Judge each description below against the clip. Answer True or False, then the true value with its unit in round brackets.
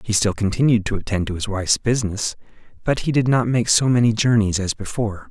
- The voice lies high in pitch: False (110 Hz)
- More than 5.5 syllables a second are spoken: True (6.1 syllables/s)